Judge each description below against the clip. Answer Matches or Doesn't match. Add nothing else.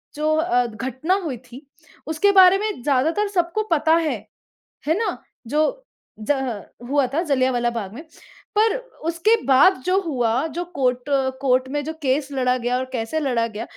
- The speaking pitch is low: Doesn't match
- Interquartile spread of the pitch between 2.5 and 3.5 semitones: Doesn't match